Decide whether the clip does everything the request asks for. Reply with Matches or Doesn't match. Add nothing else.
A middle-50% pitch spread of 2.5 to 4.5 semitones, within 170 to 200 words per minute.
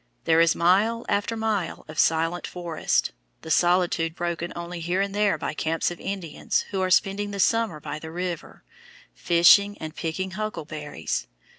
Doesn't match